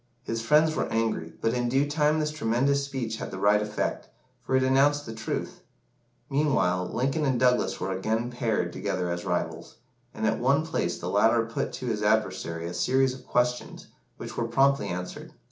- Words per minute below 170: No, average, 185 wpm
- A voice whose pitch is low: Yes, low, 115 Hz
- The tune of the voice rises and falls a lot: No, average, 4.7 semitones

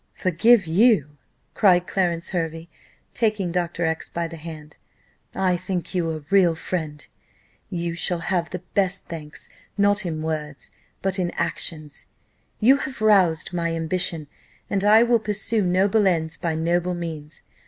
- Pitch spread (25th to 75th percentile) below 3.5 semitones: Yes, average, 3.1 semitones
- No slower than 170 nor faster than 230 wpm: No, average, 145 wpm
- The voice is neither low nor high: Yes, medium, 175 Hz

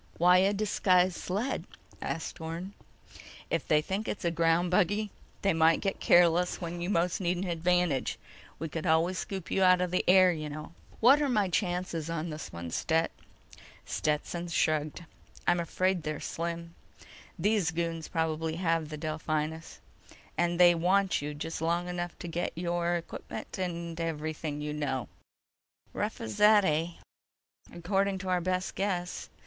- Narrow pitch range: Yes, narrow, 2.2 semitones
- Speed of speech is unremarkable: Yes, average, 155 wpm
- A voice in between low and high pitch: Yes, medium, 170 Hz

